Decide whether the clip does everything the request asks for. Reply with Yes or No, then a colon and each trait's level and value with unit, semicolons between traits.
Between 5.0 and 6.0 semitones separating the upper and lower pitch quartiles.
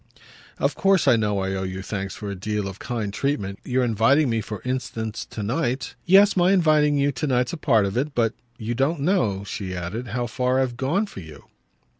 Yes: wide, 5.6 semitones